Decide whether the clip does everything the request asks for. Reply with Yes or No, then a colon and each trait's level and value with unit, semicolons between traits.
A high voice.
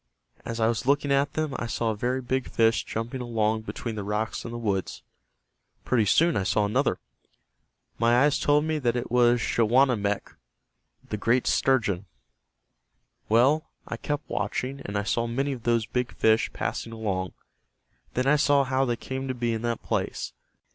No: low, 120 Hz